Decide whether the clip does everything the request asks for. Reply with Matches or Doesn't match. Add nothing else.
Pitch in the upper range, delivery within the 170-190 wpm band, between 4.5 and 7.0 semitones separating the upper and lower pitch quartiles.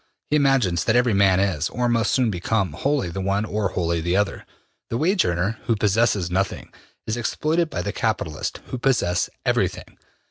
Doesn't match